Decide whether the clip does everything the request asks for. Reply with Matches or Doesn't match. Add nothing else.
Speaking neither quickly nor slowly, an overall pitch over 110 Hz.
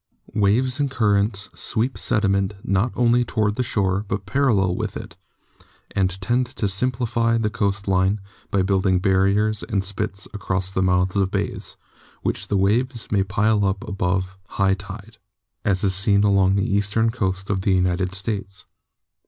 Doesn't match